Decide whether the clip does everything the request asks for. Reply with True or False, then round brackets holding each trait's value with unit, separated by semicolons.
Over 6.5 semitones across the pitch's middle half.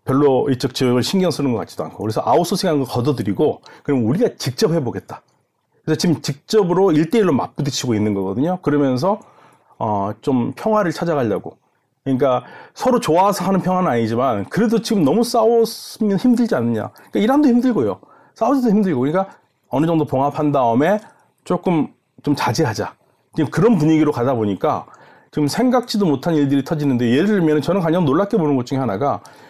True (7.6 semitones)